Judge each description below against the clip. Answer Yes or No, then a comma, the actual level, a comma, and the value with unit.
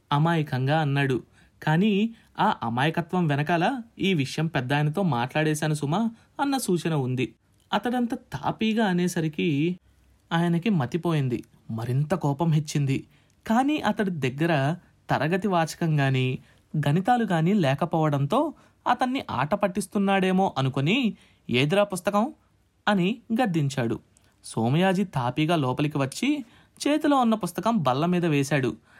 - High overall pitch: No, medium, 170 Hz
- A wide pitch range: Yes, wide, 6.5 semitones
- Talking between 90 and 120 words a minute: Yes, average, 100 wpm